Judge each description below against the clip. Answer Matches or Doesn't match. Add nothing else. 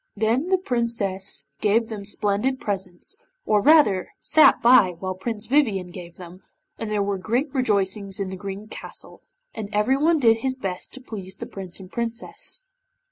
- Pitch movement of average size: Matches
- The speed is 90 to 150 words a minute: Doesn't match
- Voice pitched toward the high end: Matches